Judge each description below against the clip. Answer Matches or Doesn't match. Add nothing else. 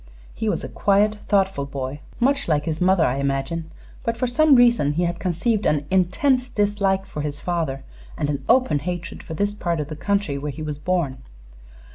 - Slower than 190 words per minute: Doesn't match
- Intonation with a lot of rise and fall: Matches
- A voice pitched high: Doesn't match